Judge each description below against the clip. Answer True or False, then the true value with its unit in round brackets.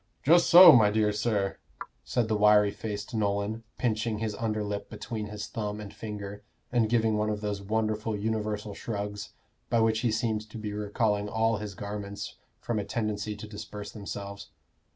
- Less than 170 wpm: False (175 wpm)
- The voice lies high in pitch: False (105 Hz)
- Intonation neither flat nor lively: False (1.3 semitones)